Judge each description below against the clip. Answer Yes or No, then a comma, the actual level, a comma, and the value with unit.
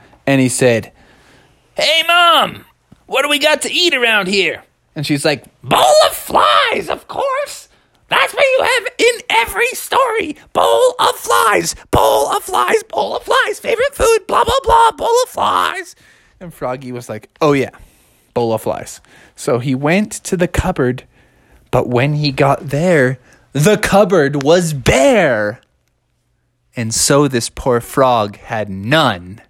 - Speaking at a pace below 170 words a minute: Yes, average, 155 wpm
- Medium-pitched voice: Yes, medium, 155 Hz